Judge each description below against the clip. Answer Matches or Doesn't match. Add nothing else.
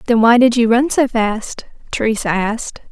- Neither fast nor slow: Matches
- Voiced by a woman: Matches